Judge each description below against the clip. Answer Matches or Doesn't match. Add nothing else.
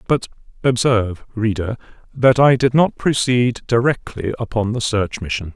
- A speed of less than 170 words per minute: Matches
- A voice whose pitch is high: Doesn't match